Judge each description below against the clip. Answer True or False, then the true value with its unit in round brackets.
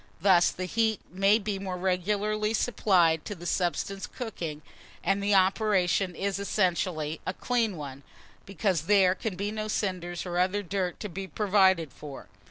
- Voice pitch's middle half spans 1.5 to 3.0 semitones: True (2.7 semitones)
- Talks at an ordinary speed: True (160 wpm)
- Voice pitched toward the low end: False (190 Hz)